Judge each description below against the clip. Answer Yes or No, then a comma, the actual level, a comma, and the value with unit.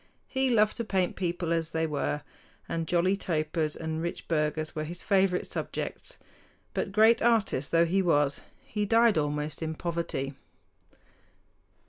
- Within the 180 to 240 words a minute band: No, average, 145 wpm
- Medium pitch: Yes, medium, 170 Hz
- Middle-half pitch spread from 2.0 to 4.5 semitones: Yes, average, 4.0 semitones